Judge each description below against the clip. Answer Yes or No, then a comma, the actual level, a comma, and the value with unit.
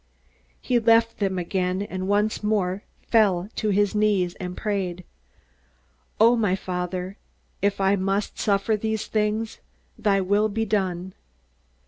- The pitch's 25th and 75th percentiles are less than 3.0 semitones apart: Yes, narrow, 2.4 semitones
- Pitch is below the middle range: No, high, 200 Hz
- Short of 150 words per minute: Yes, slow, 135 wpm